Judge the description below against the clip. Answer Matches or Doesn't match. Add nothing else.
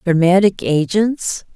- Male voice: Doesn't match